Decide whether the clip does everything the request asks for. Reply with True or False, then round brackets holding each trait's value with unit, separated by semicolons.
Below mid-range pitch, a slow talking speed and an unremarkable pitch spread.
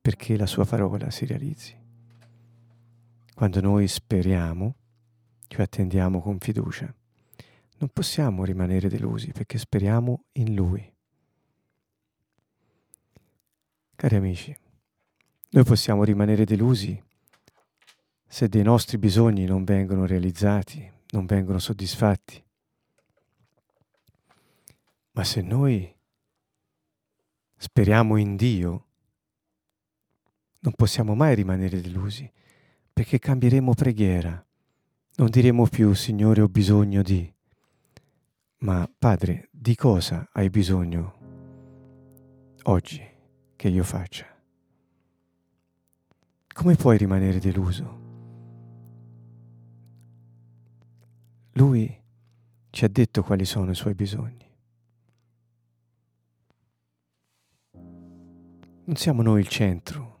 True (110 Hz; 85 wpm; 3.9 semitones)